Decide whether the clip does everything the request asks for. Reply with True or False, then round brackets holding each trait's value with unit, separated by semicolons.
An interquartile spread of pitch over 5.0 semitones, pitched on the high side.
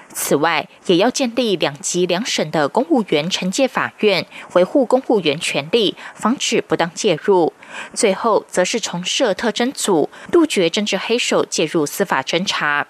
True (5.6 semitones; 195 Hz)